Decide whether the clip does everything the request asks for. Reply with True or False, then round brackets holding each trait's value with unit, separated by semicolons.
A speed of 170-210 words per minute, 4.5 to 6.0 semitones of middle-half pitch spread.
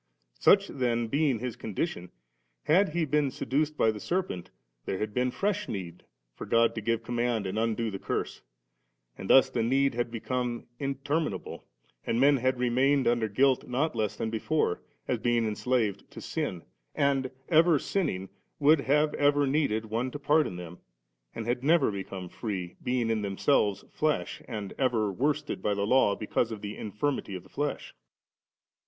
True (175 wpm; 4.9 semitones)